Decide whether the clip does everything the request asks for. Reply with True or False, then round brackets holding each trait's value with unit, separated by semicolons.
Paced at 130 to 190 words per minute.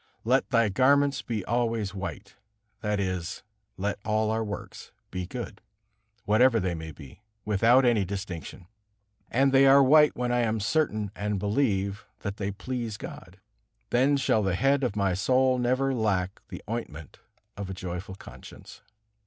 True (155 wpm)